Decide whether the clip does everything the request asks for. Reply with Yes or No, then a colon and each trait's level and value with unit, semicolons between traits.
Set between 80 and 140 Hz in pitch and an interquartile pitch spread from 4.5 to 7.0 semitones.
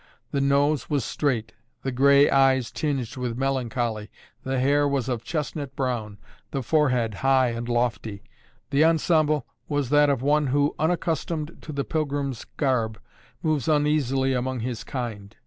No: low, 135 Hz; average, 3.1 semitones